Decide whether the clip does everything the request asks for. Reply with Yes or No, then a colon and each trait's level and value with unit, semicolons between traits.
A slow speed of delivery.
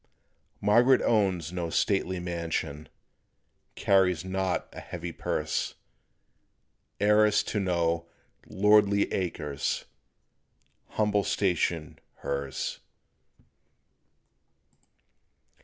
Yes: slow, 70 wpm